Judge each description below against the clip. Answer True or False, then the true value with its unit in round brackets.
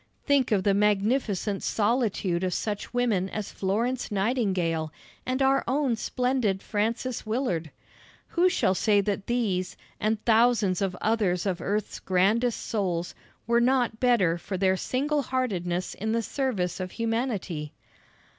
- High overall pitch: True (215 Hz)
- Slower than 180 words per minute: True (135 wpm)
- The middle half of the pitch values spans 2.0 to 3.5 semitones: False (4.5 semitones)